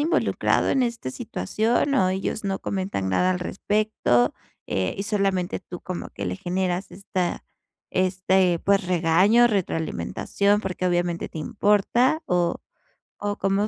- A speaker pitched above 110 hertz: Yes, high, 190 Hz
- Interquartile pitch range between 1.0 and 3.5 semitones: Yes, average, 2.7 semitones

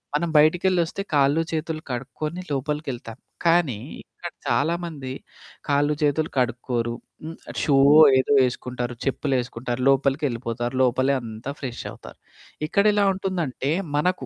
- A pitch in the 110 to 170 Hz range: Yes, medium, 140 Hz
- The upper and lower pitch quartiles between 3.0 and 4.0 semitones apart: No, average, 4.4 semitones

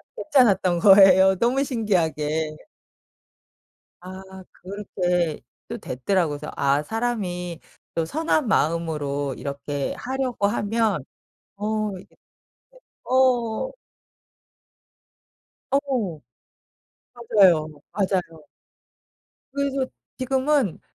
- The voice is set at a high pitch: Yes, high, 195 Hz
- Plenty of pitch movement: Yes, wide, 6.9 semitones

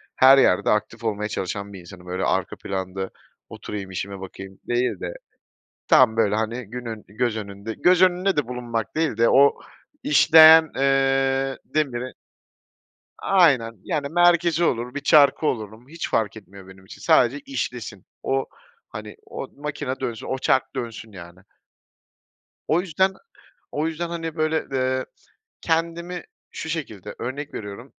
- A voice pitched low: Yes, low, 125 Hz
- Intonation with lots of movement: Yes, wide, 6.6 semitones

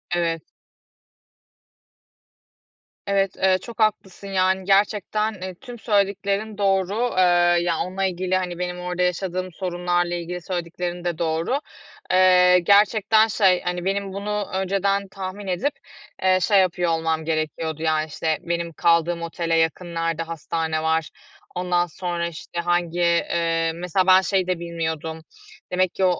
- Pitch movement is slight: Yes, narrow, 2.3 semitones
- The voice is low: No, medium, 180 Hz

